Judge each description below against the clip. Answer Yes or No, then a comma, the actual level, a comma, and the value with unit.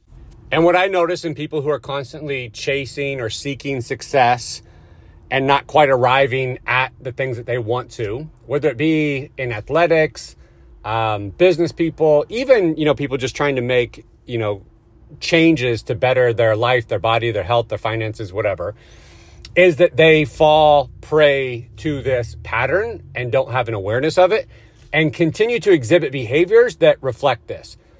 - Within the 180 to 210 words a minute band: No, average, 165 wpm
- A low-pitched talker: Yes, low, 130 Hz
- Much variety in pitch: No, average, 5.0 semitones